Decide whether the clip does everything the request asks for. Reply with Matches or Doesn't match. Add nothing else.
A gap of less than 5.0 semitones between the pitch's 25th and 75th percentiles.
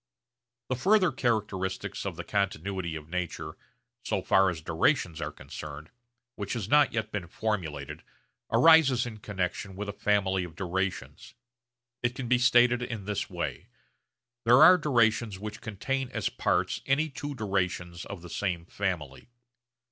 Doesn't match